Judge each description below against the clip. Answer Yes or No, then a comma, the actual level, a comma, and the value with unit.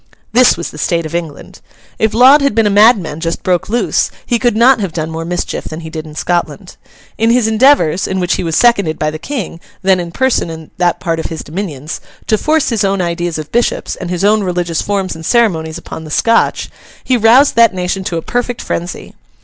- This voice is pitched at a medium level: Yes, medium, 180 Hz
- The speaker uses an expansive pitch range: Yes, wide, 5.7 semitones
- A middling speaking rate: No, fast, 220 wpm